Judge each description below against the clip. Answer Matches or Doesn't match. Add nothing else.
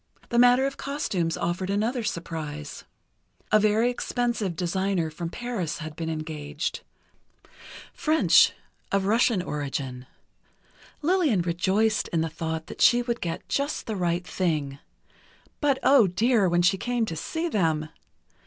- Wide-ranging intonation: Matches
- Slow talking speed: Matches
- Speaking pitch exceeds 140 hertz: Matches